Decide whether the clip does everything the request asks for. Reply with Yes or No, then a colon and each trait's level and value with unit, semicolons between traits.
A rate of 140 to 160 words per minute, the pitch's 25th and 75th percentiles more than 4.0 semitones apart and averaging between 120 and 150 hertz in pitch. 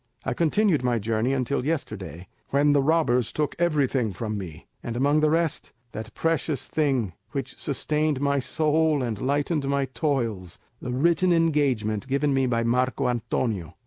Yes: average, 155 wpm; average, 4.4 semitones; low, 135 Hz